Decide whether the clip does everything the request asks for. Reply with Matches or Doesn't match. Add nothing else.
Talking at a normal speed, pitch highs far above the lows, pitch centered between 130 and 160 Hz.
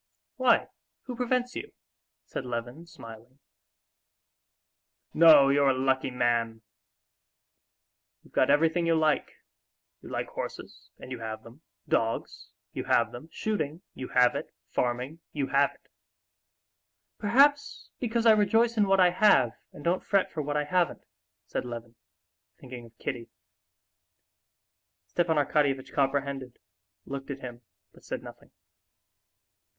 Doesn't match